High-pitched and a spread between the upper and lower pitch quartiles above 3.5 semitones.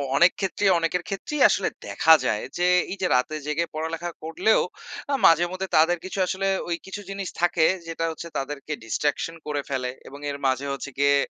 No: medium, 165 Hz; average, 4.0 semitones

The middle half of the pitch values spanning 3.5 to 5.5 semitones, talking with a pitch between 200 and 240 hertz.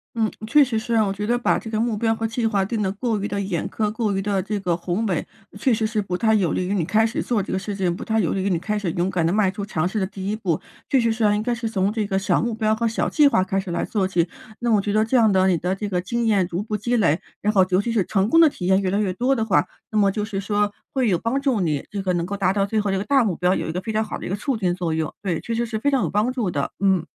No: average, 2.9 semitones; high, 205 Hz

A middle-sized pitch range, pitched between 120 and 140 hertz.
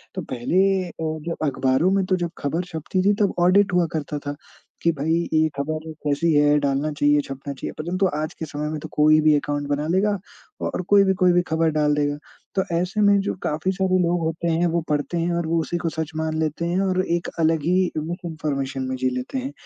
No: average, 3.2 semitones; medium, 160 Hz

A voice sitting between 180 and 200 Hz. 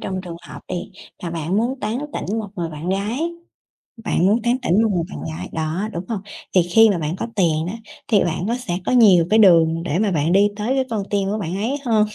Yes: high, 190 Hz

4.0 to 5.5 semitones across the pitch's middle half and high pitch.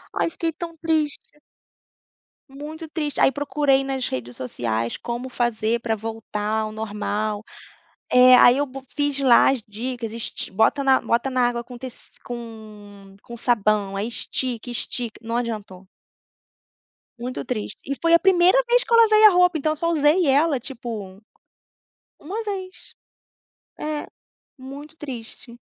Yes: average, 5.2 semitones; very high, 250 Hz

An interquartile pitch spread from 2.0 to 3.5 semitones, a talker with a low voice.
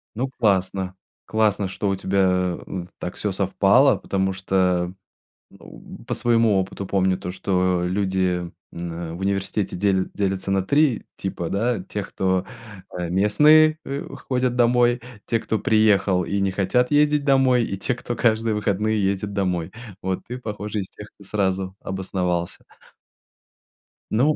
Yes: average, 3.2 semitones; low, 100 Hz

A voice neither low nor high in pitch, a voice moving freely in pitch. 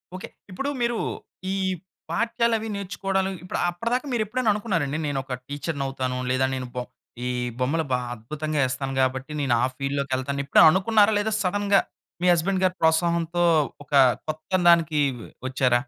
Yes: medium, 165 Hz; wide, 6.5 semitones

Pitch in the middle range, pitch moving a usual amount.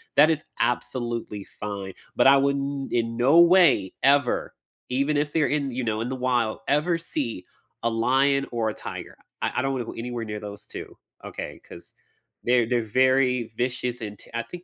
No: low, 125 Hz; average, 3.3 semitones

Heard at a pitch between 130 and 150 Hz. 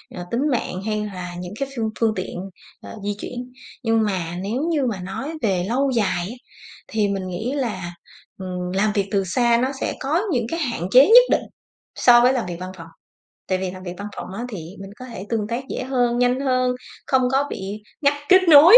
No: high, 225 Hz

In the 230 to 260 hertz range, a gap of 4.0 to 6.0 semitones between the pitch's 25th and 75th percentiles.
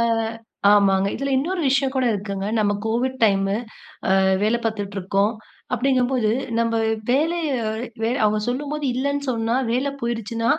Yes: high, 235 Hz; average, 4.4 semitones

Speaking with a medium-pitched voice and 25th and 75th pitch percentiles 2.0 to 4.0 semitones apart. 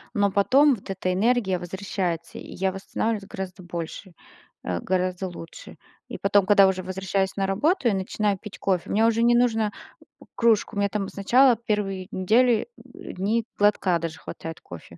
No: high, 195 Hz; average, 2.9 semitones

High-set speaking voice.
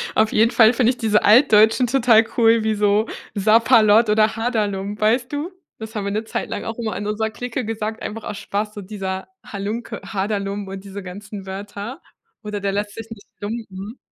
Yes: high, 215 Hz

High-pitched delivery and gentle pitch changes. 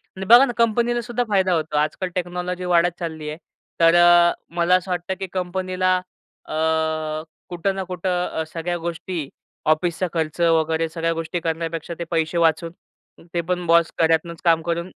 No: medium, 170 Hz; narrow, 2.0 semitones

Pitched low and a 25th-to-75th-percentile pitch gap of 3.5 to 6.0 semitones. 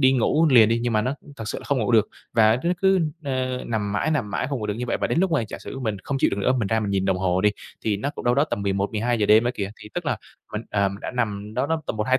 Yes: low, 115 Hz; average, 3.9 semitones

